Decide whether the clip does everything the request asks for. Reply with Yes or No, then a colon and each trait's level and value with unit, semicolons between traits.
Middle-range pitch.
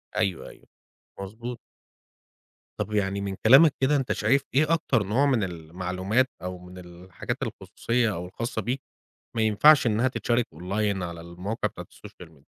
No: low, 105 Hz